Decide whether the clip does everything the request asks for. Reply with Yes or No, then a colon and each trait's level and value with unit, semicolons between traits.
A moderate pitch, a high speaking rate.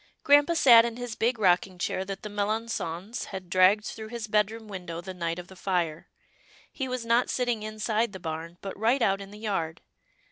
No: high, 210 Hz; fast, 210 wpm